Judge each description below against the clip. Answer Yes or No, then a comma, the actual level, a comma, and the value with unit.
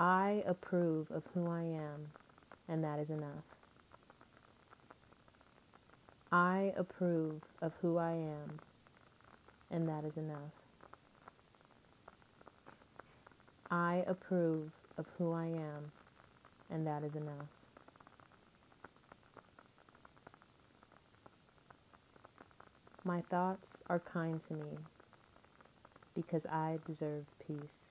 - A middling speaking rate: No, slow, 85 wpm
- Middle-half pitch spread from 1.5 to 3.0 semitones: Yes, narrow, 2.5 semitones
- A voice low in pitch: No, medium, 160 Hz